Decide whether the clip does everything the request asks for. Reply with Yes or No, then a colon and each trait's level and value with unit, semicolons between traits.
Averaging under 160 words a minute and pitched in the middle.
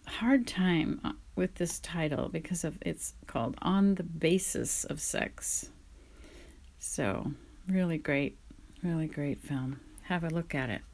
Yes: slow, 135 wpm; medium, 160 Hz